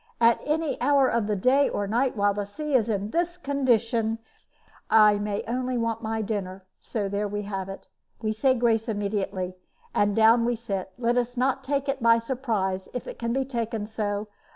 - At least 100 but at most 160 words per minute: No, average, 185 wpm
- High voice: Yes, high, 225 Hz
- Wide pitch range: No, average, 3.3 semitones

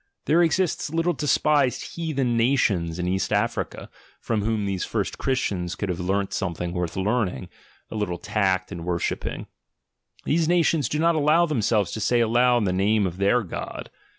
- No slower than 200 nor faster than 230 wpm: No, average, 170 wpm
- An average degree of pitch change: No, wide, 7.7 semitones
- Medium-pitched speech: No, low, 110 Hz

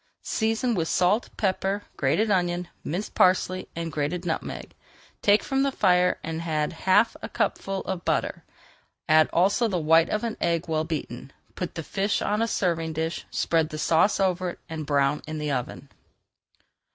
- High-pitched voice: No, medium, 175 Hz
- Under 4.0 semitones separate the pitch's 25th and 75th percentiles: Yes, average, 3.5 semitones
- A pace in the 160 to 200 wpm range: Yes, average, 170 wpm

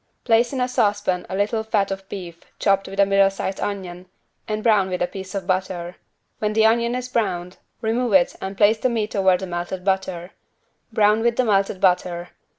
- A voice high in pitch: Yes, high, 195 Hz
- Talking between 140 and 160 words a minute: No, average, 195 wpm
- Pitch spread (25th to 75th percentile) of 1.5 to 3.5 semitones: Yes, average, 2.9 semitones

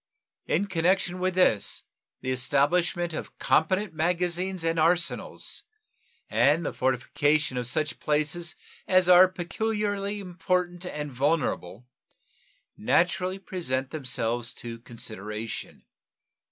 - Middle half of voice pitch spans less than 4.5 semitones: No, wide, 5.6 semitones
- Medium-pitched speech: Yes, medium, 165 Hz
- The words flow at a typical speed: No, slow, 100 wpm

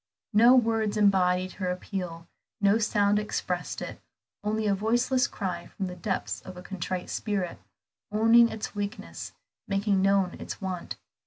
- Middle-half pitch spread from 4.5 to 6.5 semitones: No, average, 2.7 semitones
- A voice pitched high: Yes, high, 200 Hz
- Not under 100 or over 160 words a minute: Yes, average, 145 wpm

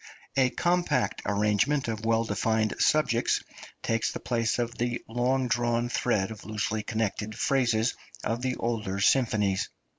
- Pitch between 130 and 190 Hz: No, low, 115 Hz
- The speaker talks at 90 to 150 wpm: Yes, average, 140 wpm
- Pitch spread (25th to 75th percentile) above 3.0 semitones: No, narrow, 2.4 semitones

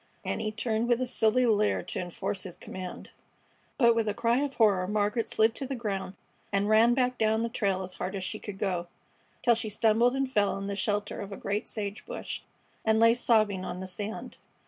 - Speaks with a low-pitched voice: No, high, 215 Hz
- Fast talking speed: Yes, fast, 215 wpm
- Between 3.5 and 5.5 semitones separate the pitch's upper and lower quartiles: No, average, 2.8 semitones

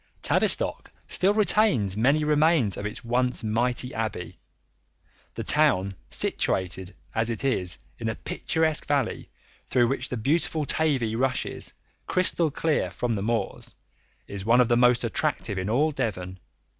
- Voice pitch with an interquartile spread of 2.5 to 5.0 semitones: No, wide, 5.5 semitones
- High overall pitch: No, low, 120 Hz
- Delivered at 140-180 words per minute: Yes, average, 145 wpm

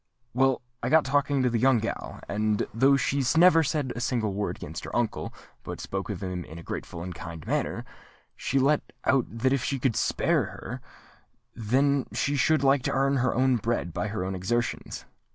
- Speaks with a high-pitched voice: No, low, 125 Hz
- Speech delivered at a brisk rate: No, average, 195 wpm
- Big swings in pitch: No, average, 4.3 semitones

